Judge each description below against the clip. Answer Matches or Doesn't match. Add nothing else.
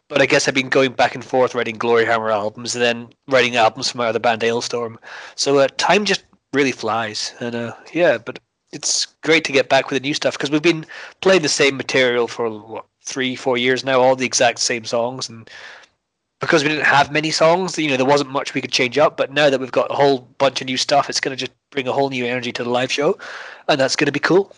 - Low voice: Matches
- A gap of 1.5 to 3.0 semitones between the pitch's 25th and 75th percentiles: Matches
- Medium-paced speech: Doesn't match